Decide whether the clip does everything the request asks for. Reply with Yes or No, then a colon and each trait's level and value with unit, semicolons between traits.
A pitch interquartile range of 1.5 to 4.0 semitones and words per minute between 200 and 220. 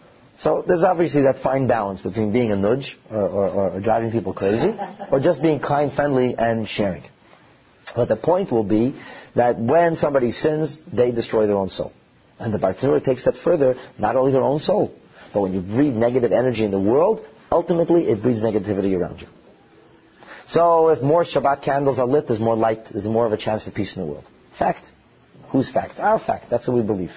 No: average, 5.0 semitones; fast, 205 wpm